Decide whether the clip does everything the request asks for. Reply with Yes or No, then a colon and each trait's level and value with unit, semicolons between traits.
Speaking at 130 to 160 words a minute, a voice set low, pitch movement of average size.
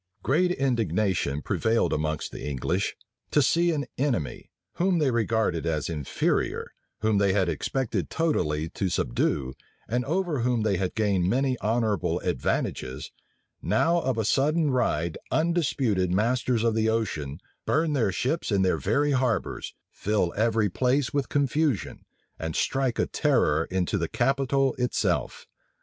No: average, 155 wpm; low, 115 Hz; wide, 6.8 semitones